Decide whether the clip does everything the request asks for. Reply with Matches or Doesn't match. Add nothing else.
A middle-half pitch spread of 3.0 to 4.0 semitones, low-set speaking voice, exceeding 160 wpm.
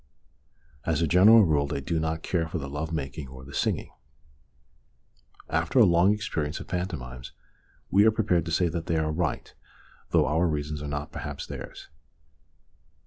Matches